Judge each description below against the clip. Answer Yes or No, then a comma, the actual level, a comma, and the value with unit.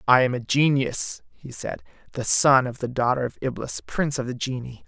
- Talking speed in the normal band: No, fast, 210 wpm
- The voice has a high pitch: No, low, 130 Hz